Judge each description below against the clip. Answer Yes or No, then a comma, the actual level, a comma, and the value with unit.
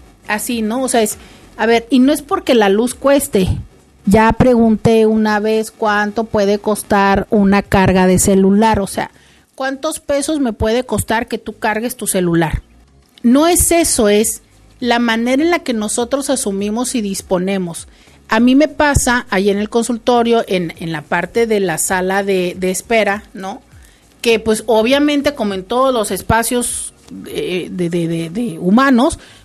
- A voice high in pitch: Yes, high, 220 Hz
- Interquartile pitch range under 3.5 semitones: No, average, 3.8 semitones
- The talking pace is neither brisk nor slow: Yes, average, 170 wpm